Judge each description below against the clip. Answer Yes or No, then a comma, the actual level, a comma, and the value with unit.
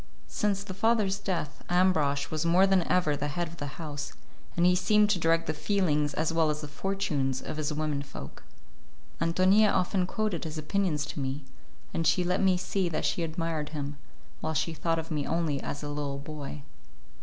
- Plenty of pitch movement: No, average, 3.8 semitones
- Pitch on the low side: No, medium, 165 Hz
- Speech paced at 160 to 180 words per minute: No, average, 195 wpm